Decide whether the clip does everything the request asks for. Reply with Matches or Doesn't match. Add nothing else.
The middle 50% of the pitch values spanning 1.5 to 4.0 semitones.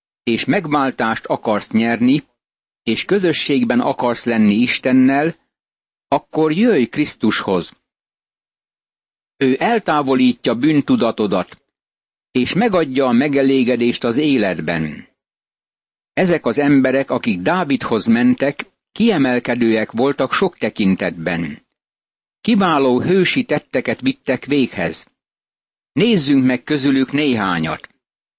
Doesn't match